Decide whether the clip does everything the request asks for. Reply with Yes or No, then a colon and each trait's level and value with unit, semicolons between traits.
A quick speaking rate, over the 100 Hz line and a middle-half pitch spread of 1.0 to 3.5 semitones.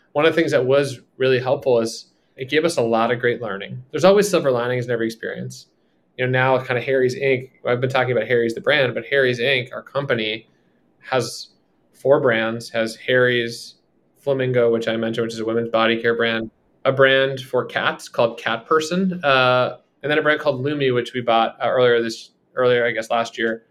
Yes: fast, 210 wpm; low, 125 Hz; average, 2.7 semitones